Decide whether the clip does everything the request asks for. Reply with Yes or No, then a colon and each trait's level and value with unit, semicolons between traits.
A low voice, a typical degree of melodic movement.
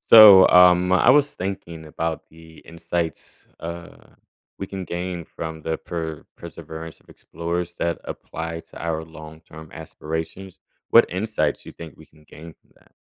No: very low, 85 Hz; narrow, 2.0 semitones